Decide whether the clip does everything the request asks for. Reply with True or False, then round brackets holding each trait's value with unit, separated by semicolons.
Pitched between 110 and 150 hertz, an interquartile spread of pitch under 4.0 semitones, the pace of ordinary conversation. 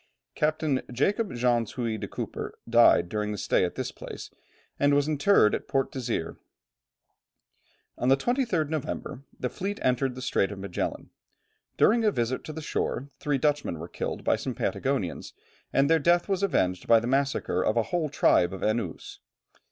False (135 Hz; 5.2 semitones; 175 wpm)